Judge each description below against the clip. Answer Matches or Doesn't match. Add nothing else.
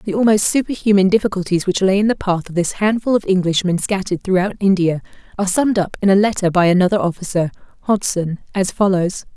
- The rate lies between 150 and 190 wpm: Matches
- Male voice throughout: Doesn't match